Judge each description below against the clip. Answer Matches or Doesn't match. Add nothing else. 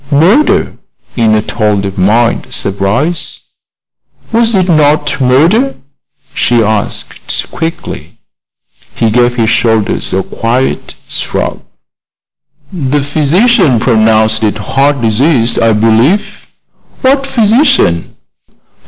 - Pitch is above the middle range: Doesn't match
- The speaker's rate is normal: Doesn't match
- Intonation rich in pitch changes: Matches